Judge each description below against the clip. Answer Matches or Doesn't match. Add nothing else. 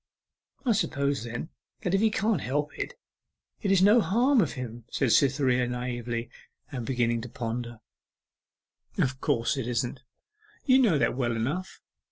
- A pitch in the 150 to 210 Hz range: Doesn't match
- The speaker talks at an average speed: Matches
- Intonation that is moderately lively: Doesn't match